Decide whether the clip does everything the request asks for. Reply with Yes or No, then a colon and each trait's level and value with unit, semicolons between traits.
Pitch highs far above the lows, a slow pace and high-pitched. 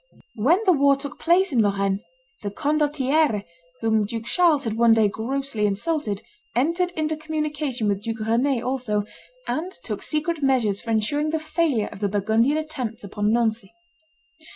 No: wide, 5.9 semitones; average, 155 wpm; very high, 250 Hz